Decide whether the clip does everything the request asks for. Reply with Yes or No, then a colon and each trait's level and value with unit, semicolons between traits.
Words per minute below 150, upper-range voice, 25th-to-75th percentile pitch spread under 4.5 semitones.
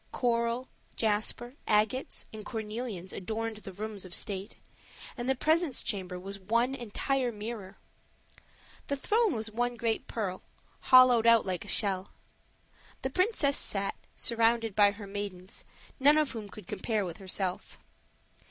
Yes: slow, 135 wpm; high, 220 Hz; average, 3.6 semitones